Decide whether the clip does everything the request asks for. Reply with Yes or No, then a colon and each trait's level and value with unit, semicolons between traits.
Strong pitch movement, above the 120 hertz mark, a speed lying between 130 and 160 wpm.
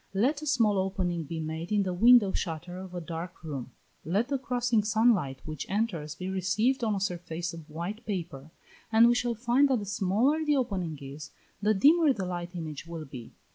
No: wide, 5.7 semitones; high, 190 Hz; fast, 205 wpm